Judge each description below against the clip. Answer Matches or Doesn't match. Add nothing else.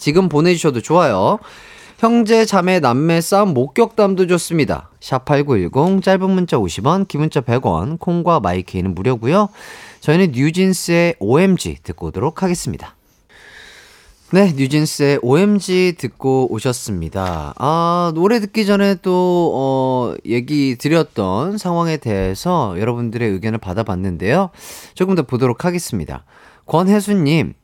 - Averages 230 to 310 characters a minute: Matches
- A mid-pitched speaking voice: Matches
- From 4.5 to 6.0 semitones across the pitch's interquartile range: Doesn't match